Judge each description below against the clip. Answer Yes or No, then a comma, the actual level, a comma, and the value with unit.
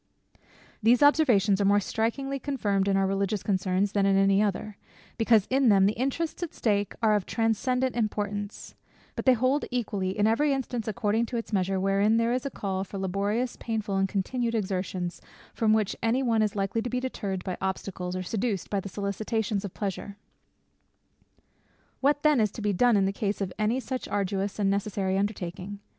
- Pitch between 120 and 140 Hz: No, high, 205 Hz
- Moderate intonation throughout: Yes, average, 3.1 semitones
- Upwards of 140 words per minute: Yes, average, 185 wpm